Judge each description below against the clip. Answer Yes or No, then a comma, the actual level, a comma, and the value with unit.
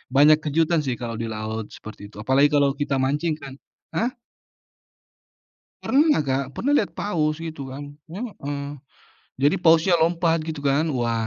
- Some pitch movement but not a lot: Yes, average, 3.8 semitones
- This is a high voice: No, medium, 145 Hz